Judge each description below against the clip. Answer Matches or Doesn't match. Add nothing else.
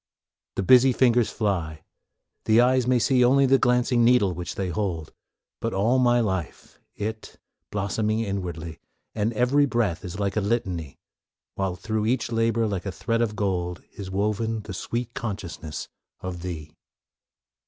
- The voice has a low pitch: Matches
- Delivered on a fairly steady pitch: Doesn't match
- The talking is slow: Doesn't match